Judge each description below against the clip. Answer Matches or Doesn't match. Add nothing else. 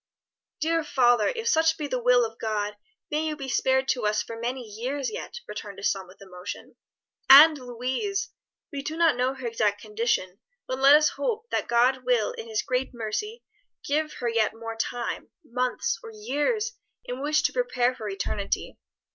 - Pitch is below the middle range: Doesn't match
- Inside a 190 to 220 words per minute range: Doesn't match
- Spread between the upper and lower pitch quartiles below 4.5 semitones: Doesn't match